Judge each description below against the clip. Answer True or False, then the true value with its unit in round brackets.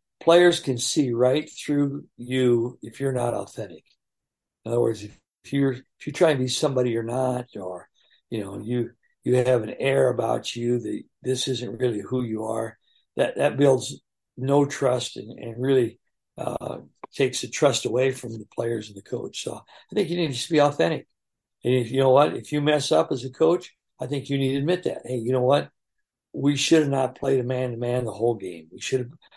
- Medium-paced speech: False (215 wpm)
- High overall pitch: False (130 Hz)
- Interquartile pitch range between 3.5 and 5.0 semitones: False (2.9 semitones)